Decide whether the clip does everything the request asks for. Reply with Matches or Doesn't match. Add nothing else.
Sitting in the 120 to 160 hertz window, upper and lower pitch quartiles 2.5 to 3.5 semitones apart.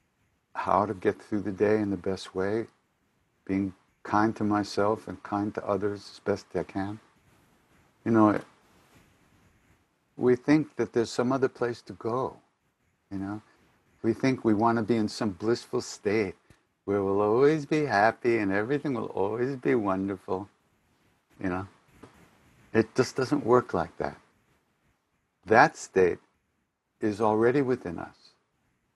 Doesn't match